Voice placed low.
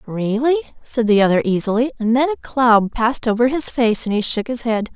No: high, 235 Hz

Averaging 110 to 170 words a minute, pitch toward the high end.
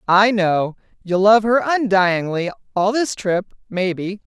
Yes: average, 140 wpm; high, 200 Hz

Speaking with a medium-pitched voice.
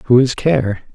No: low, 125 Hz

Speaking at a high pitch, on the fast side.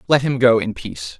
No: low, 120 Hz; fast, 250 wpm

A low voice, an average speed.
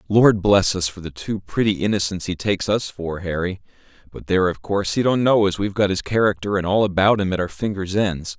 No: very low, 95 Hz; fast, 235 wpm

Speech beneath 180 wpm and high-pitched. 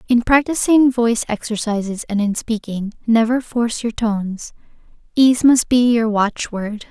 Yes: average, 140 wpm; high, 230 Hz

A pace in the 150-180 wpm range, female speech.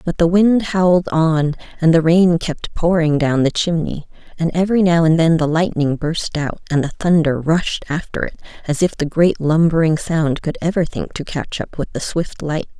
No: fast, 205 wpm; female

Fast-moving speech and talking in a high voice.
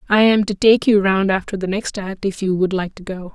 Yes: fast, 285 wpm; high, 195 Hz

